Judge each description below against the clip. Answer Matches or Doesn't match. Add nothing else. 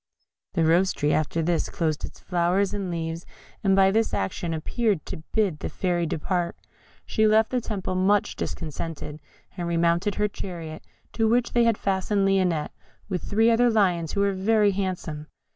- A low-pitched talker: Doesn't match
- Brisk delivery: Doesn't match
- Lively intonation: Doesn't match